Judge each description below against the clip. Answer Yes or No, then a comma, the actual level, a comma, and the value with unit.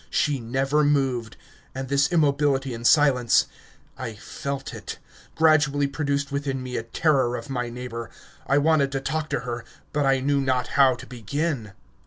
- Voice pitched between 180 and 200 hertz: No, low, 135 Hz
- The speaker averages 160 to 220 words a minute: Yes, average, 165 wpm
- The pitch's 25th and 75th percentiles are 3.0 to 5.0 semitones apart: No, narrow, 2.6 semitones